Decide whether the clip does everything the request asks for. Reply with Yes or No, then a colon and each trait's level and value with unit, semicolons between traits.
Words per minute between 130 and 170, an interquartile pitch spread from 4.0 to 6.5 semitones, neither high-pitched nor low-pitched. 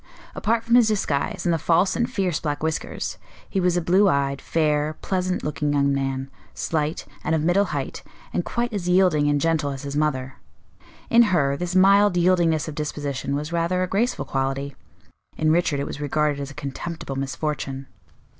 No: average, 185 wpm; average, 4.3 semitones; medium, 155 Hz